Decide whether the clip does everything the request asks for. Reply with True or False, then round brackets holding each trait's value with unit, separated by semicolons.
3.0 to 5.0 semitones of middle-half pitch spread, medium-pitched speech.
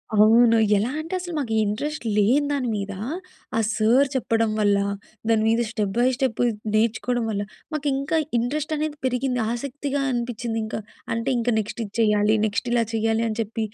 False (3.5 semitones; 235 Hz)